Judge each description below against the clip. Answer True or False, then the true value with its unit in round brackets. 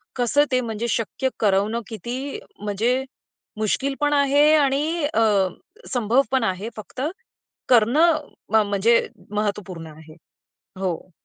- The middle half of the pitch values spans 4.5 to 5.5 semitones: True (4.8 semitones)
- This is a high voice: True (230 Hz)